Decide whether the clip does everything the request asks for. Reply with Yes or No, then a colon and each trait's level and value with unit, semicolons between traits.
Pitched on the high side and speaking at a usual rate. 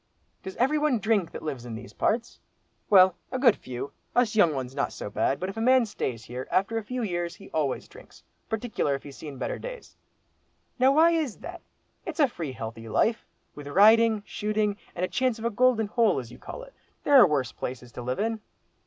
No: high, 205 Hz; fast, 215 wpm